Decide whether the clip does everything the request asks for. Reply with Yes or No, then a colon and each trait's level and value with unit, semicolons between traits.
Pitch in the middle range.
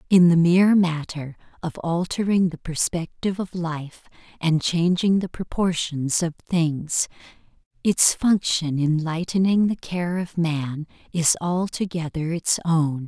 Yes: medium, 170 Hz